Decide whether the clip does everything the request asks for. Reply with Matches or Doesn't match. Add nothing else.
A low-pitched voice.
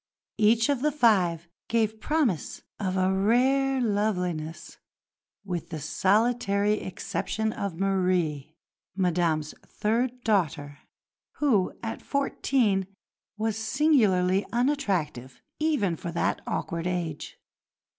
Doesn't match